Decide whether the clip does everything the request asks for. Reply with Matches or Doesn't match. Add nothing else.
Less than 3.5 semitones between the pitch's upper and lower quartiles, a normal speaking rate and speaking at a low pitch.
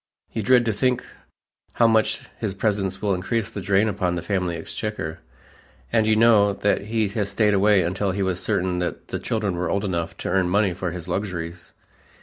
Matches